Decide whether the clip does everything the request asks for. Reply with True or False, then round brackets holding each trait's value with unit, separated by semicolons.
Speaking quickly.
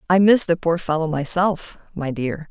False (190 wpm)